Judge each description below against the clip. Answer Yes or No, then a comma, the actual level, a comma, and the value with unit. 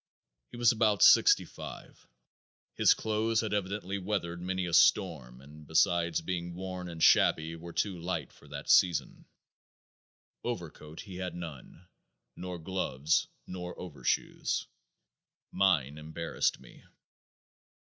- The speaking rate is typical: No, slow, 120 wpm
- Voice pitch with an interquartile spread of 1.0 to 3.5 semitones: Yes, average, 2.8 semitones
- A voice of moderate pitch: No, very low, 90 Hz